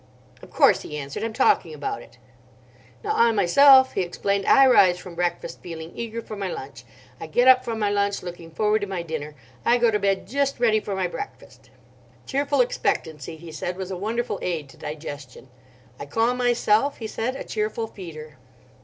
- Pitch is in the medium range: No, high, 200 Hz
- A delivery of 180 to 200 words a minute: Yes, average, 190 wpm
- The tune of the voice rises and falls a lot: Yes, wide, 5.9 semitones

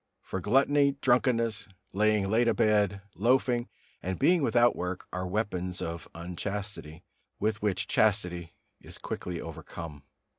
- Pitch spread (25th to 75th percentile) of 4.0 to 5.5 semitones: Yes, average, 4.5 semitones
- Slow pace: Yes, slow, 120 wpm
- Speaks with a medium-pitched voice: No, low, 105 Hz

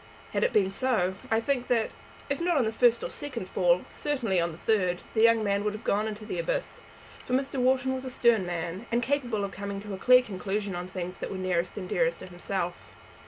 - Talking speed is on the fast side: Yes, fast, 240 wpm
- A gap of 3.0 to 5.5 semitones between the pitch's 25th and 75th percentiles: Yes, average, 5.0 semitones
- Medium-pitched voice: No, high, 220 Hz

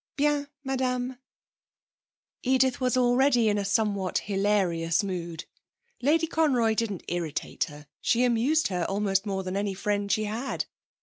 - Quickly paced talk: No, slow, 135 wpm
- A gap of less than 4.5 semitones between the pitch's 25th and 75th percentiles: No, average, 4.8 semitones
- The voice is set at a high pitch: Yes, high, 215 Hz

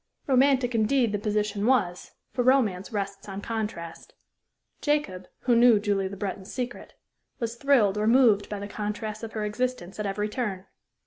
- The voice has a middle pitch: No, high, 210 Hz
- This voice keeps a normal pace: Yes, average, 165 wpm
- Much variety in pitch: No, average, 3.4 semitones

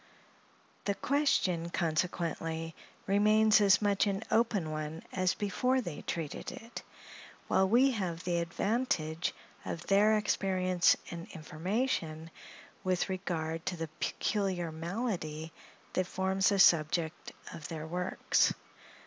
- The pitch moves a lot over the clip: No, average, 3.7 semitones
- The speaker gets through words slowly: Yes, slow, 115 wpm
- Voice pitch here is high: No, medium, 180 Hz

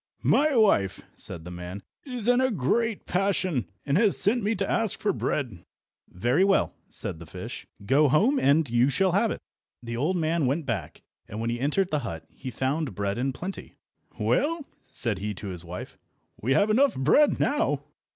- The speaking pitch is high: No, medium, 150 Hz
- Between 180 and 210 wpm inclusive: Yes, average, 190 wpm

